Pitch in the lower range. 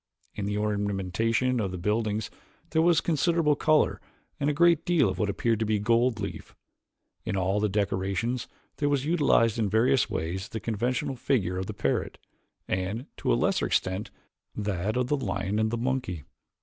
Yes: low, 110 Hz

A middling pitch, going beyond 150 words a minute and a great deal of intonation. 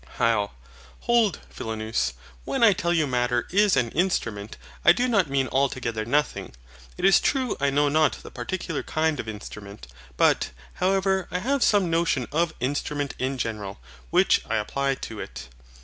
Yes: medium, 145 Hz; average, 165 wpm; wide, 7.9 semitones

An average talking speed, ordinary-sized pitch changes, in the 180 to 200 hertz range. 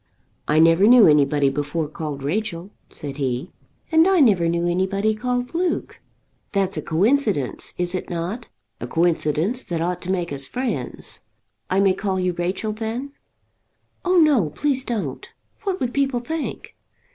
No: average, 155 wpm; wide, 7.0 semitones; medium, 185 Hz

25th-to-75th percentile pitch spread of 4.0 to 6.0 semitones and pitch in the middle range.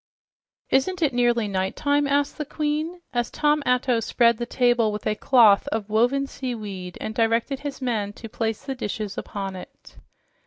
No: average, 4.5 semitones; high, 240 Hz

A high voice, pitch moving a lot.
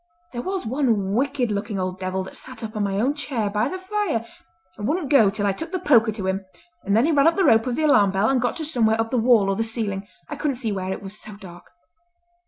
Yes: high, 225 Hz; wide, 5.7 semitones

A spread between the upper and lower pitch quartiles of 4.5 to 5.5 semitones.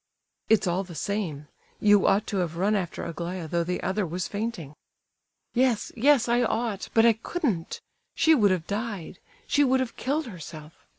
Yes: average, 5.2 semitones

